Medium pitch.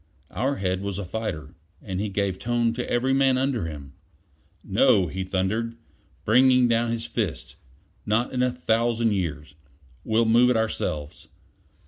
No: low, 110 Hz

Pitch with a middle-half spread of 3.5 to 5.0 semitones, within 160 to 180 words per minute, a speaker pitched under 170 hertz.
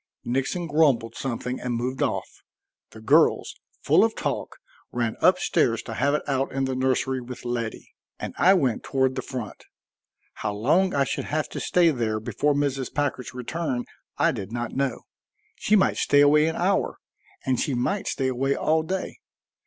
Yes: average, 3.8 semitones; average, 175 wpm; low, 135 Hz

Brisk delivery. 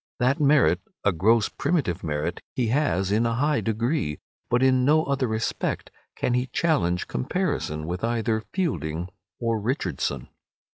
No: average, 145 wpm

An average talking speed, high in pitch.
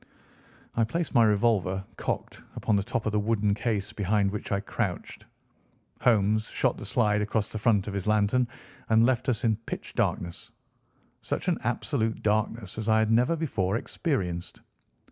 No: average, 165 wpm; low, 110 Hz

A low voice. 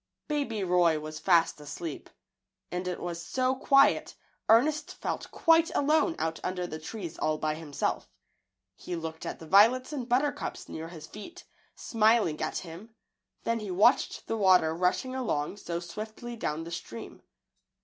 No: medium, 185 Hz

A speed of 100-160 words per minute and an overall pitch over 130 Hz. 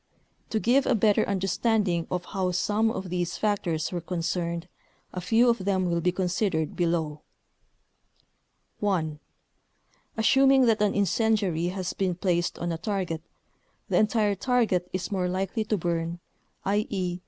Yes: average, 140 wpm; medium, 185 Hz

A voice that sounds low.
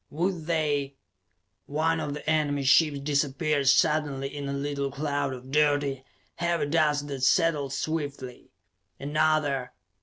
No: medium, 145 Hz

